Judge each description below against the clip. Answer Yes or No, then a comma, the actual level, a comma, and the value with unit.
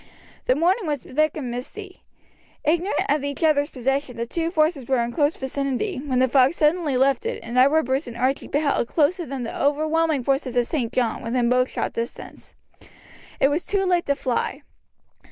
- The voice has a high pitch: Yes, very high, 280 Hz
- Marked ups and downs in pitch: No, average, 3.7 semitones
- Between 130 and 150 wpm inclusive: No, average, 185 wpm